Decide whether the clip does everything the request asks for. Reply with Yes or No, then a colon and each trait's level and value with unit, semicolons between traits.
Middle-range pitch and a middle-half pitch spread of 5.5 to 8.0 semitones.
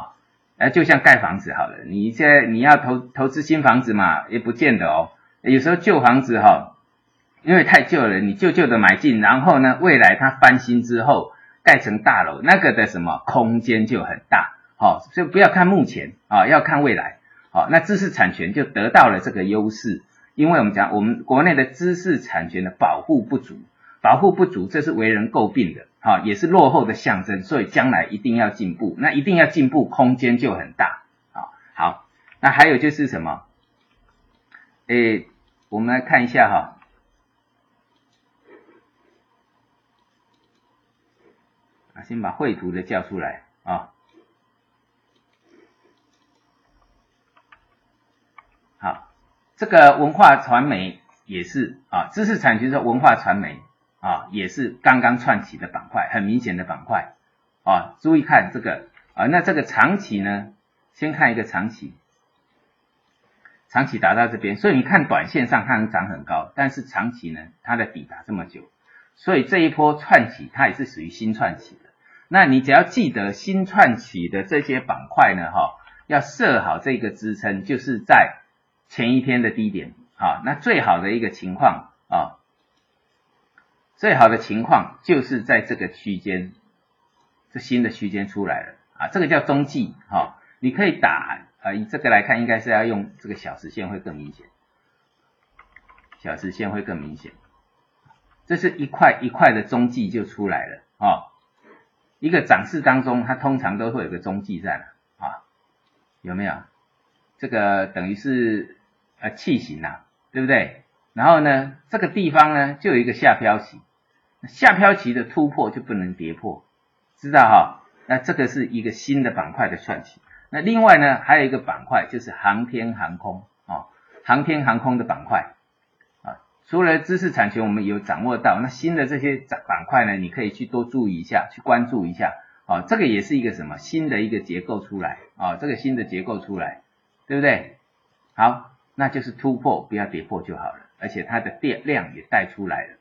No: low, 120 Hz; wide, 5.8 semitones